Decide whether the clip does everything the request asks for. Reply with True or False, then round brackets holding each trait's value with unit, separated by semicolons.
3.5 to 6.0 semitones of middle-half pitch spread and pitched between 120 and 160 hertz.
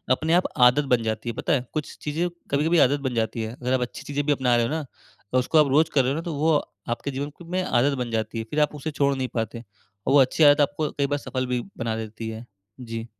True (3.9 semitones; 135 Hz)